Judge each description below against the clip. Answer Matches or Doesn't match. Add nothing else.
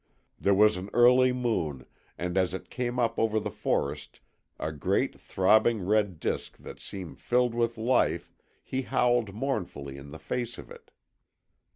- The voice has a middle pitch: Doesn't match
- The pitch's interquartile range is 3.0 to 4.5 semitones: Doesn't match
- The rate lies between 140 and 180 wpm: Matches